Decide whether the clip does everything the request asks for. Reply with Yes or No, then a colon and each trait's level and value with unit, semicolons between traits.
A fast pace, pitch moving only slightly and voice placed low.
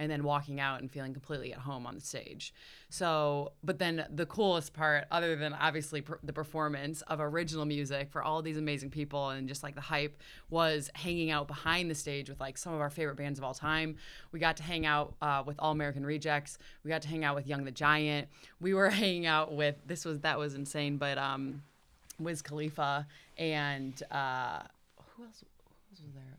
No: fast, 215 wpm; narrow, 1.8 semitones; medium, 150 Hz